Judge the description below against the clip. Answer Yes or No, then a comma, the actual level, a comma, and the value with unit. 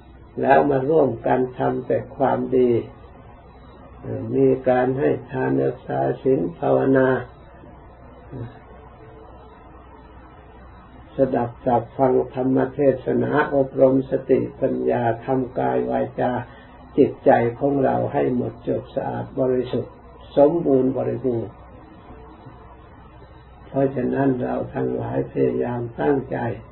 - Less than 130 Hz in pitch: Yes, low, 120 Hz